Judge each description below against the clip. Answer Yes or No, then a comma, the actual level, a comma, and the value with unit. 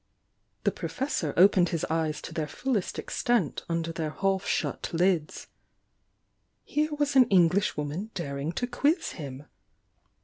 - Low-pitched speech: No, medium, 175 Hz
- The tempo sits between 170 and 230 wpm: No, average, 140 wpm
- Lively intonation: Yes, wide, 6.2 semitones